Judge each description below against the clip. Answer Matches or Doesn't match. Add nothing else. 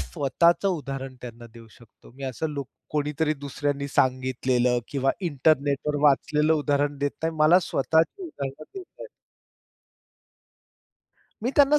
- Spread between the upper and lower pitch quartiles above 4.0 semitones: Doesn't match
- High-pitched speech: Doesn't match